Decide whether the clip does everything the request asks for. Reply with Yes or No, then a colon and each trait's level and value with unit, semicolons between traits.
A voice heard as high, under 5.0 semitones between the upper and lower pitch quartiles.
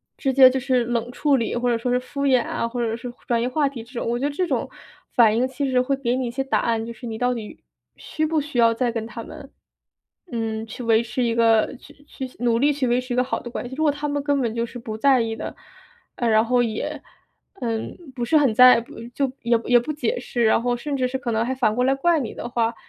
Yes: high, 245 Hz; narrow, 2.6 semitones